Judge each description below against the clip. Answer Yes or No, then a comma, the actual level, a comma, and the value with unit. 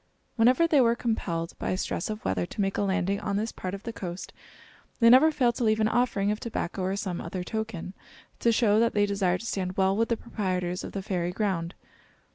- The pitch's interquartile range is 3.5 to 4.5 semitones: Yes, average, 3.8 semitones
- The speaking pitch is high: Yes, high, 200 Hz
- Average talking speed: No, fast, 225 wpm